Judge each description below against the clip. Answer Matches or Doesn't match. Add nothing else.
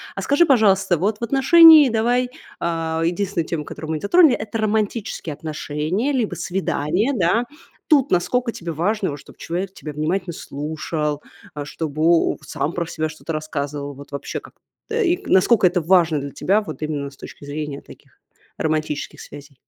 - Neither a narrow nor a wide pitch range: Doesn't match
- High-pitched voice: Doesn't match